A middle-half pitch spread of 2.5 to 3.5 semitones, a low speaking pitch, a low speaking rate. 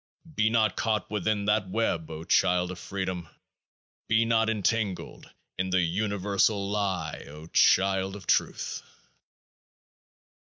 Yes: average, 2.8 semitones; low, 100 Hz; slow, 120 wpm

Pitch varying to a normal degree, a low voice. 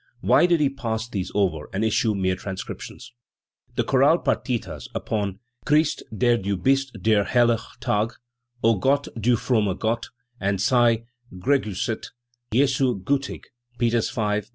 Yes: average, 4.3 semitones; low, 115 Hz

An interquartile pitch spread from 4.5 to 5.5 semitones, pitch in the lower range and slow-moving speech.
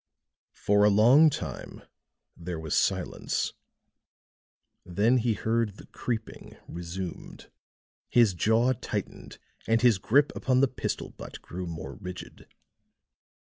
Yes: average, 5.0 semitones; low, 110 Hz; slow, 115 wpm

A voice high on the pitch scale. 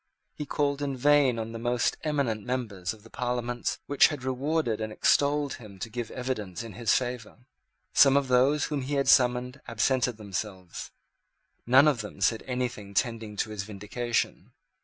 No: low, 125 Hz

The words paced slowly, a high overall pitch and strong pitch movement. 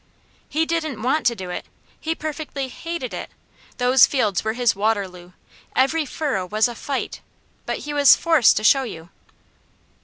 No: average, 160 wpm; very high, 255 Hz; wide, 5.8 semitones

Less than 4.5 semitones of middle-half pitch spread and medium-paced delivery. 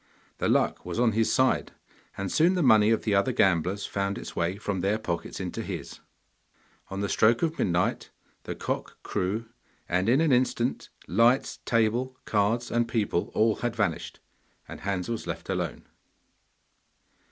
Yes: average, 3.3 semitones; average, 165 wpm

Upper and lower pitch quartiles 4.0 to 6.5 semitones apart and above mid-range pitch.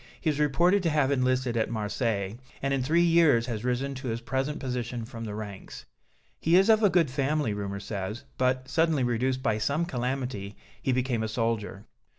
No: average, 4.3 semitones; low, 130 Hz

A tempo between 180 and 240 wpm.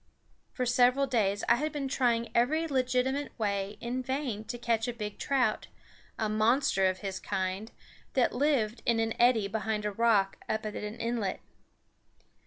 No: average, 165 wpm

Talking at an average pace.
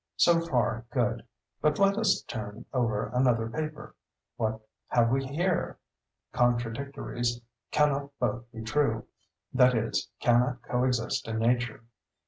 No: slow, 110 wpm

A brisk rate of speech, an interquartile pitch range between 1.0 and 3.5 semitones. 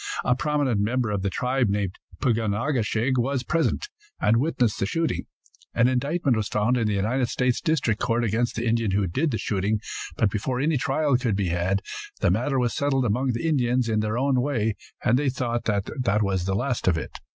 No: fast, 215 wpm; average, 3.9 semitones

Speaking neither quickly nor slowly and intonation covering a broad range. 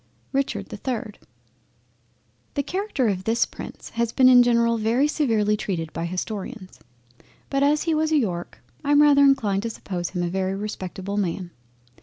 Yes: average, 170 wpm; wide, 6.3 semitones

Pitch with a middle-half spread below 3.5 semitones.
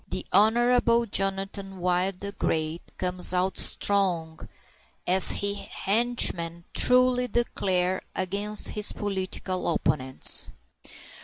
Yes: narrow, 2.6 semitones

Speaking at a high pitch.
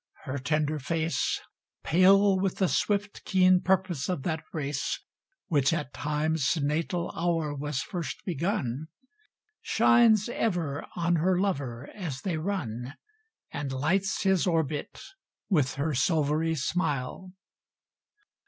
No: medium, 160 Hz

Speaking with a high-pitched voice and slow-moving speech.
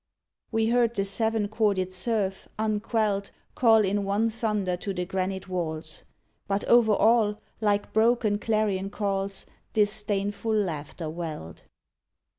Yes: high, 205 Hz; slow, 120 wpm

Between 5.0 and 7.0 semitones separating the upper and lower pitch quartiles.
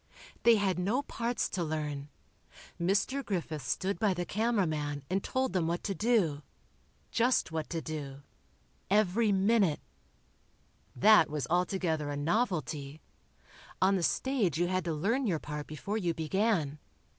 Yes: wide, 5.5 semitones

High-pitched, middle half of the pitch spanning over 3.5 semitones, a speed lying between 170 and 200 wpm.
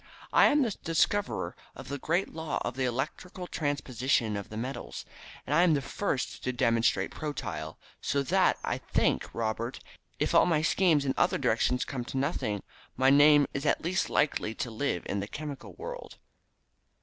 No: medium, 140 Hz; average, 4.8 semitones; average, 175 wpm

